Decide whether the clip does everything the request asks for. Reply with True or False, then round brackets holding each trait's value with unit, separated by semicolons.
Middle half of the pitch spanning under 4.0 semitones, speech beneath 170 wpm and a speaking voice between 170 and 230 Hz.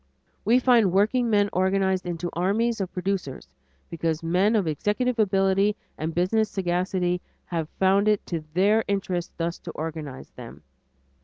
True (3.3 semitones; 140 wpm; 190 Hz)